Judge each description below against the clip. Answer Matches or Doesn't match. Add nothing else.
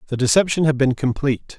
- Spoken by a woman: Doesn't match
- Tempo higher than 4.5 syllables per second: Matches